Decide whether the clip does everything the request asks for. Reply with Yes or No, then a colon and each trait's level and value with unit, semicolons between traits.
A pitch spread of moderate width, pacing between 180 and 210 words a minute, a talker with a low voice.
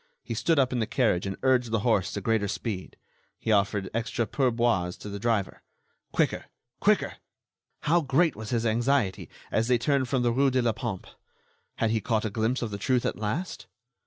Yes: average, 3.5 semitones; average, 195 wpm; low, 115 Hz